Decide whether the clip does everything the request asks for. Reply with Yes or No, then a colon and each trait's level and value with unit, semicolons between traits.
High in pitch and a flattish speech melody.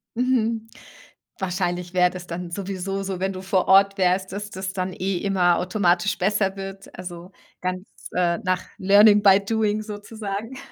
Yes: high, 195 Hz; narrow, 2.1 semitones